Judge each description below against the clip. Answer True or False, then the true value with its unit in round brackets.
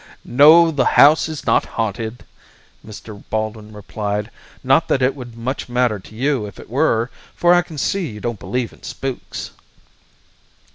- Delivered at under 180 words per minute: True (160 wpm)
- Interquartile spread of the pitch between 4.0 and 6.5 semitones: True (4.6 semitones)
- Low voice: True (125 Hz)